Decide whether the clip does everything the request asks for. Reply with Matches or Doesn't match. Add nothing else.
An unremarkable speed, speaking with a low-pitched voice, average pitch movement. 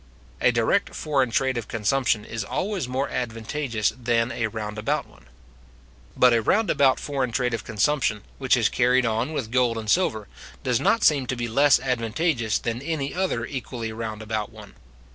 Matches